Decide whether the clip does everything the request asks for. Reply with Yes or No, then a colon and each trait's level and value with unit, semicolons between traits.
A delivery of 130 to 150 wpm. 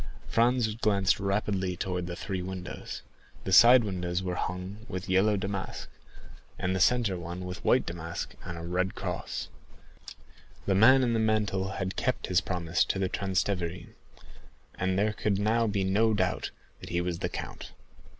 No: average, 165 wpm